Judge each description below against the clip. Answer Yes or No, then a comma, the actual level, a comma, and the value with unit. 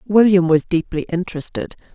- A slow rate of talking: Yes, slow, 125 wpm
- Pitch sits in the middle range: Yes, medium, 175 Hz